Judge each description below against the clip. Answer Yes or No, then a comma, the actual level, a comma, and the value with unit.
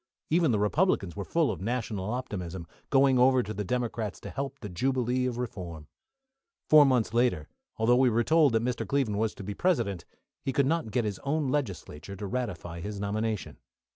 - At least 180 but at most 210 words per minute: Yes, average, 190 wpm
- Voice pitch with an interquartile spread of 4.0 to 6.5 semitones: Yes, average, 4.6 semitones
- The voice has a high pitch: No, low, 115 Hz